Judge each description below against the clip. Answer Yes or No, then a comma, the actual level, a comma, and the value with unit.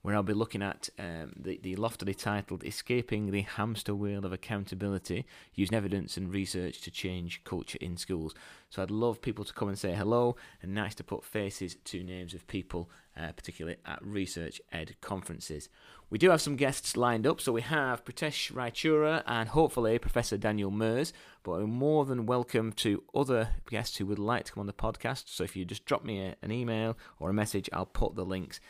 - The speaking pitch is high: No, low, 100 Hz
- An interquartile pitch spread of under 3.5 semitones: No, average, 3.8 semitones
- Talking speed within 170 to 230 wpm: Yes, fast, 205 wpm